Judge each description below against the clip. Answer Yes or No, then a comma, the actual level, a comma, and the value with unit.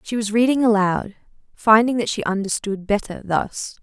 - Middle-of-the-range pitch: No, high, 215 Hz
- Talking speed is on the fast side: No, average, 155 wpm